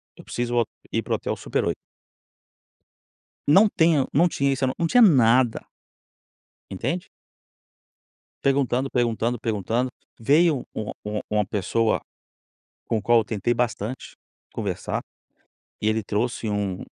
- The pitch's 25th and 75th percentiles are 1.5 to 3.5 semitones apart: No, average, 4.0 semitones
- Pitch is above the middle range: No, low, 120 Hz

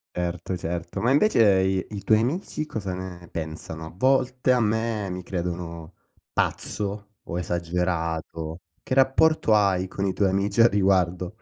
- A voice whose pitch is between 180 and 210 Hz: No, very low, 95 Hz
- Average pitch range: Yes, average, 3.9 semitones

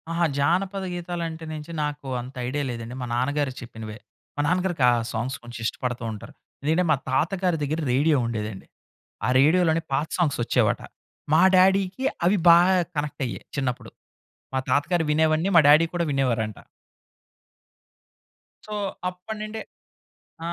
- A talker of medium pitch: Yes, medium, 155 Hz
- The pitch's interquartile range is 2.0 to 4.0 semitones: No, average, 5.3 semitones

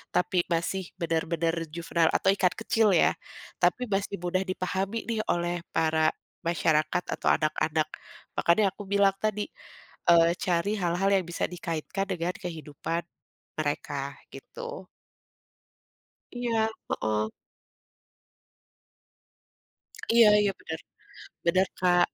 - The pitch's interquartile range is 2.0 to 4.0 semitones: Yes, average, 3.0 semitones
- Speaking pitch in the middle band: Yes, medium, 180 Hz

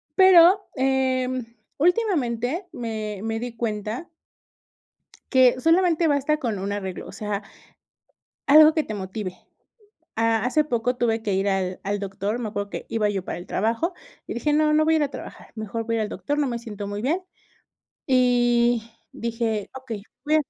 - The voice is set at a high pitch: Yes, high, 235 Hz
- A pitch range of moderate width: No, wide, 5.7 semitones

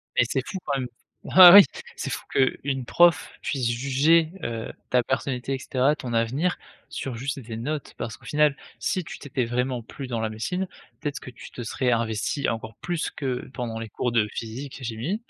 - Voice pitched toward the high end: No, low, 130 Hz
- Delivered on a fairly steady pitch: No, average, 3.8 semitones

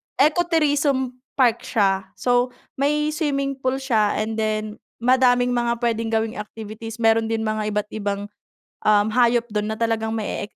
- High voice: Yes, high, 230 Hz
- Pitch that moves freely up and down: No, average, 3.1 semitones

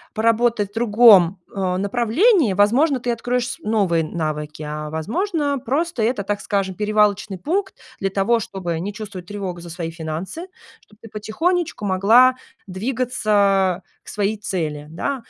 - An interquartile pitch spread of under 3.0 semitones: No, average, 4.7 semitones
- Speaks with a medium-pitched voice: No, high, 205 Hz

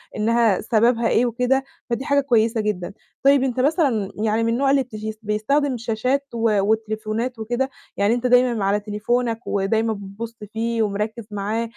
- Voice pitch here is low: No, high, 230 Hz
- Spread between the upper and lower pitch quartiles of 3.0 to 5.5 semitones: No, narrow, 2.6 semitones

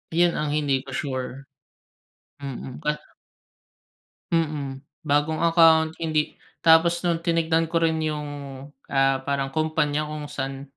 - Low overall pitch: No, medium, 155 Hz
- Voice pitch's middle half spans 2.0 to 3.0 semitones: Yes, narrow, 2.6 semitones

